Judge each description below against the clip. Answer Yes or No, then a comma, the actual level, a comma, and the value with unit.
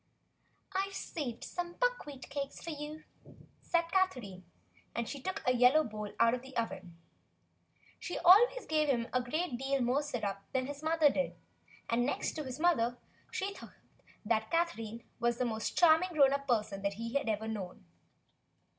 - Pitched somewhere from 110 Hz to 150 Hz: No, very high, 270 Hz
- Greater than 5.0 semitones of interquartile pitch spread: Yes, wide, 5.6 semitones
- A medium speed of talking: Yes, average, 160 wpm